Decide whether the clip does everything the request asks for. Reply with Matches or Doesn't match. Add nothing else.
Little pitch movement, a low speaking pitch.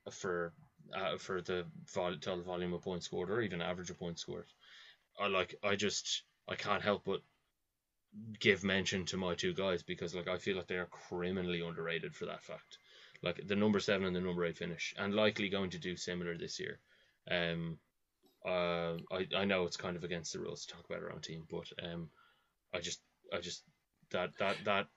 Matches